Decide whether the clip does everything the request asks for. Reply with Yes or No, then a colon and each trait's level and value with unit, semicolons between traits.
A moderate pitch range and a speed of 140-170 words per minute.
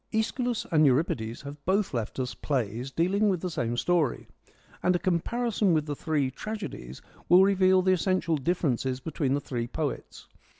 No: wide, 6.1 semitones; average, 165 wpm